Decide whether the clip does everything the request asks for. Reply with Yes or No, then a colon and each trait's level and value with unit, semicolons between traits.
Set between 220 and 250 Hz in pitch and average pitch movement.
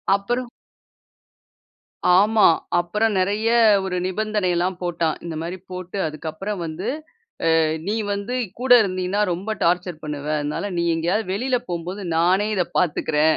No: medium, 185 Hz; average, 3.5 semitones